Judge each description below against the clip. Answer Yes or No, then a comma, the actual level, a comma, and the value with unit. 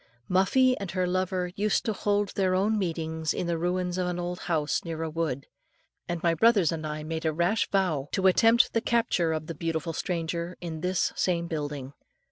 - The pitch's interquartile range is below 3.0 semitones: Yes, narrow, 2.6 semitones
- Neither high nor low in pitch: Yes, medium, 175 Hz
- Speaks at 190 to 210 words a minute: Yes, average, 195 wpm